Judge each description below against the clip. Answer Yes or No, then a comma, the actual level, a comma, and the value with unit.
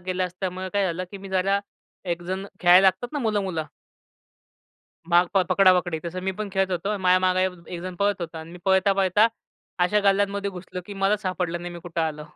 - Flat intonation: Yes, narrow, 1.8 semitones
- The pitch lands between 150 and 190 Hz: Yes, medium, 185 Hz